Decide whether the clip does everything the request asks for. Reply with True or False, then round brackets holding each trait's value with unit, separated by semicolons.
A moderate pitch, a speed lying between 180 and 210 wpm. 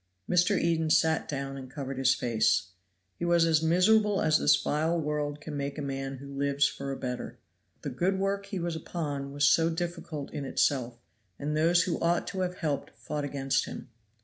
True (150 Hz; 195 wpm)